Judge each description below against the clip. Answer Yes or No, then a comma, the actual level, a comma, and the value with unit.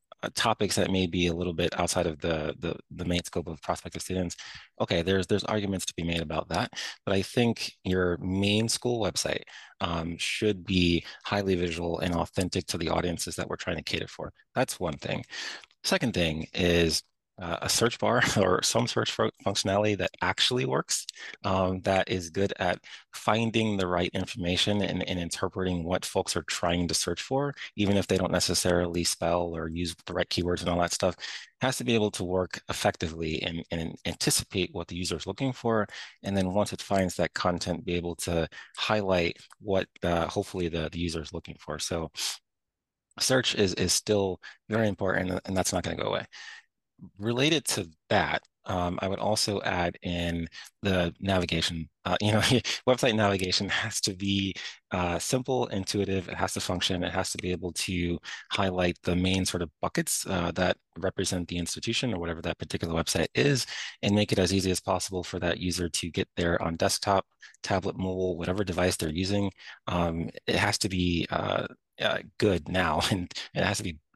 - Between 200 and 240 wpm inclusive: No, average, 190 wpm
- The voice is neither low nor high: No, very low, 90 Hz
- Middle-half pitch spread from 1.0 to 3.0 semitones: Yes, narrow, 2.5 semitones